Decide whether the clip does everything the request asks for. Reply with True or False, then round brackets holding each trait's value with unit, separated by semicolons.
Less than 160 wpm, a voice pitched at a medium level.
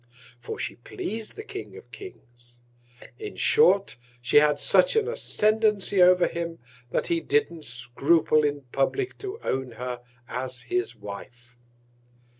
True (135 wpm; 155 Hz)